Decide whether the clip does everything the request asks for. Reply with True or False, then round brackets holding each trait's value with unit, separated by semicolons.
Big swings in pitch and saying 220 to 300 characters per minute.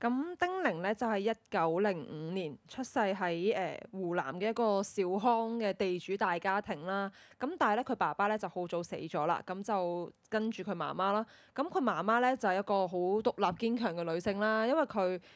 False (3.5 semitones; 295 characters per minute)